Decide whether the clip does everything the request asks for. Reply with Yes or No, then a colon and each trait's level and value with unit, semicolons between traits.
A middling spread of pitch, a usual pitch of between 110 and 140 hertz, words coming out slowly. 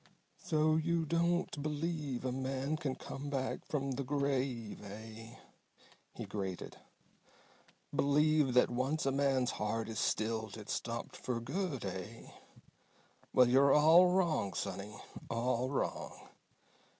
Yes: average, 4.7 semitones; low, 135 Hz; slow, 125 wpm